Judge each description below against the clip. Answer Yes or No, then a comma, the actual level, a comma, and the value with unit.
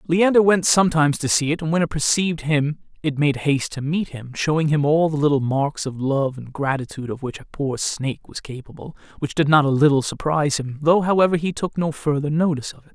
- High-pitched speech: No, medium, 150 Hz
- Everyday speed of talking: No, fast, 230 wpm